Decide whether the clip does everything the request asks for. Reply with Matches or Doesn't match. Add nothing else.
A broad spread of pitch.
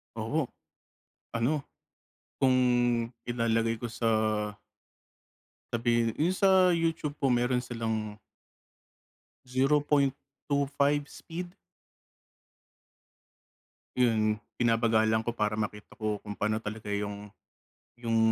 Doesn't match